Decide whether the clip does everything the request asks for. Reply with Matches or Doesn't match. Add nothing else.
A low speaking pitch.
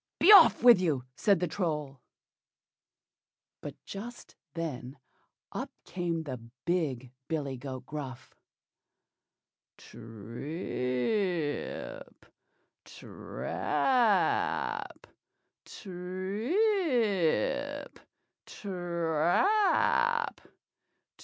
Doesn't match